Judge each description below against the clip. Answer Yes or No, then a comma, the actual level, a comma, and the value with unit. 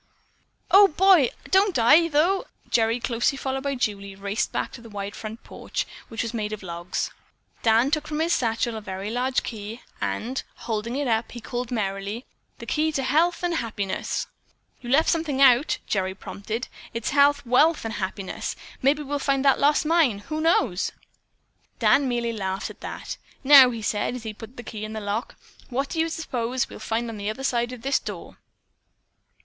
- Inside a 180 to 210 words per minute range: Yes, average, 190 wpm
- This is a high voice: Yes, high, 240 Hz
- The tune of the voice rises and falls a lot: No, average, 4.7 semitones